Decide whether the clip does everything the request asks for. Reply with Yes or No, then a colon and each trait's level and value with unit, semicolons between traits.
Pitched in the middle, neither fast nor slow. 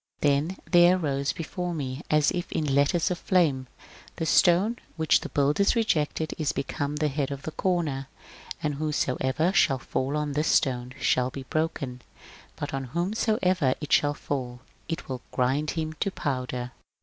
Yes: medium, 150 Hz; average, 165 wpm